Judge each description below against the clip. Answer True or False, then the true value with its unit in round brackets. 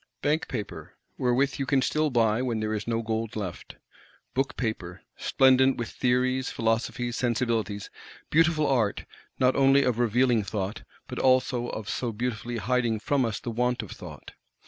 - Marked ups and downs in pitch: False (2.9 semitones)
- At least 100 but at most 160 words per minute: True (155 wpm)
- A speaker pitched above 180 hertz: False (120 Hz)